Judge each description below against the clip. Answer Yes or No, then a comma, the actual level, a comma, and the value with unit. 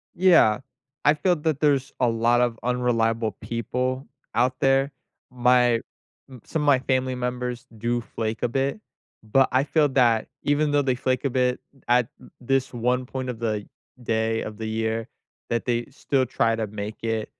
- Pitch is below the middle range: Yes, low, 125 Hz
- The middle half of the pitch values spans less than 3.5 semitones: Yes, average, 2.7 semitones